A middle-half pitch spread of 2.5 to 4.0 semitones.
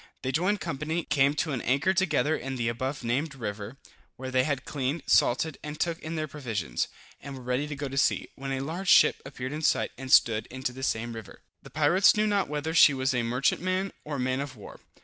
Yes: average, 3.5 semitones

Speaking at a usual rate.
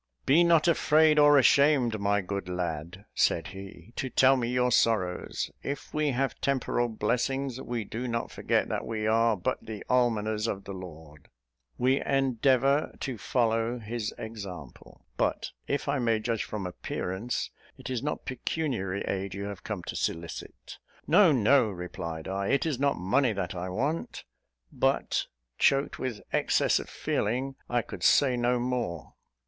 Yes: average, 160 wpm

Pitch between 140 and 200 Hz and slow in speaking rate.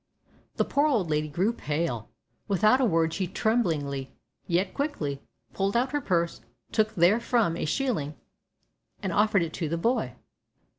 No: medium, 185 Hz; average, 150 wpm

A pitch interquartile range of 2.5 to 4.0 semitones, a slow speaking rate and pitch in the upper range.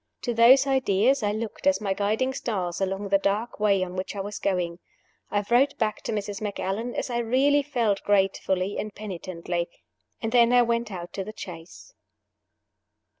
No: average, 3.6 semitones; average, 175 wpm; high, 210 Hz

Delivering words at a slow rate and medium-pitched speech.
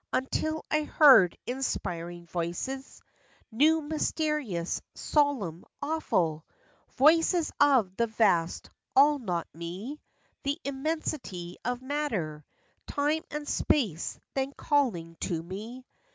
No: slow, 100 wpm; very high, 255 Hz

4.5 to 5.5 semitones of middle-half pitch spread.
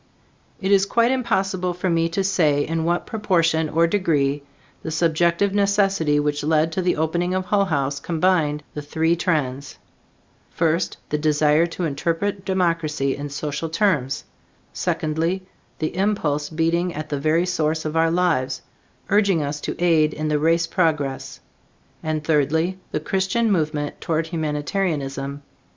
No: average, 3.3 semitones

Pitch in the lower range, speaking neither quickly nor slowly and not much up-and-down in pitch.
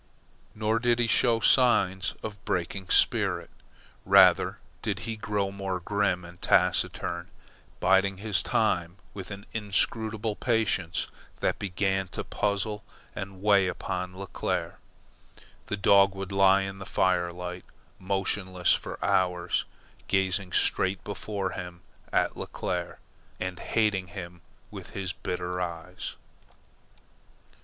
No: very low, 95 Hz; slow, 120 wpm; narrow, 2.1 semitones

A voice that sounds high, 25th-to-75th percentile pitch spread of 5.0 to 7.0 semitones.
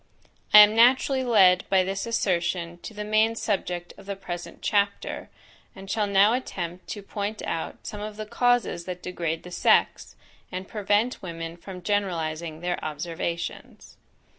No: high, 195 Hz; average, 3.3 semitones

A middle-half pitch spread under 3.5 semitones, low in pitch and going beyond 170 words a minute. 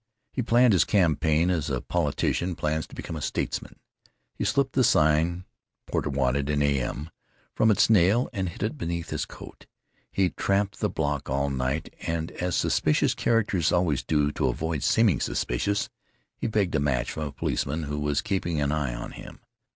No: average, 4.4 semitones; very low, 80 Hz; average, 180 wpm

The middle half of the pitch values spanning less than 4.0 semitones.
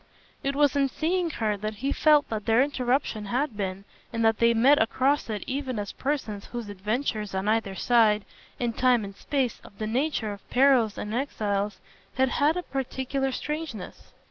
No: average, 4.6 semitones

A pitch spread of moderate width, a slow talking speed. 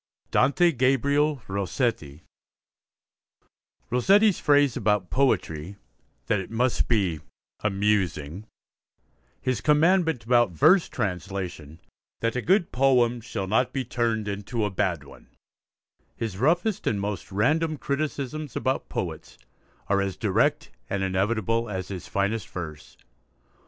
No: wide, 5.9 semitones; slow, 115 wpm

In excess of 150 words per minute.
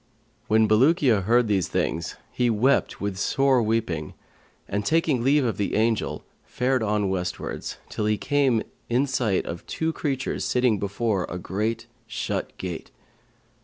No: average, 145 wpm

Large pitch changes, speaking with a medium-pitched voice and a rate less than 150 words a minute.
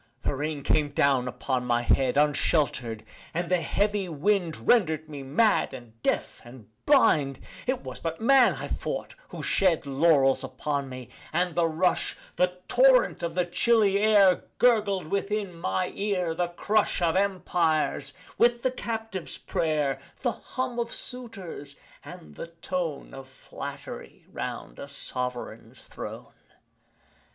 Yes: wide, 6.6 semitones; medium, 165 Hz; average, 140 wpm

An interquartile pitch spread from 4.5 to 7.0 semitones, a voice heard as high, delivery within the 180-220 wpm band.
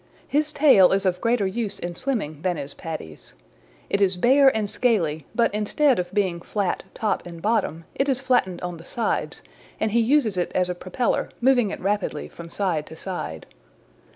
Yes: average, 5.2 semitones; high, 195 Hz; average, 185 wpm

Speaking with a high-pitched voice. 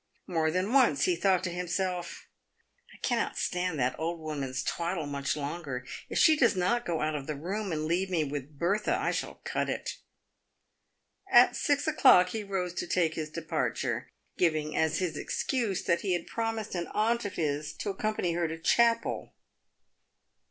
No: medium, 175 Hz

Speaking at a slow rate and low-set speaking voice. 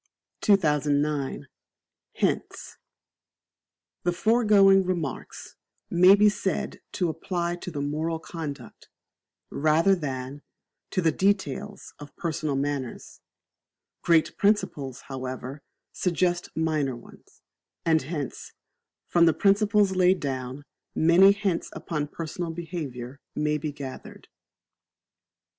No: slow, 100 wpm; medium, 160 Hz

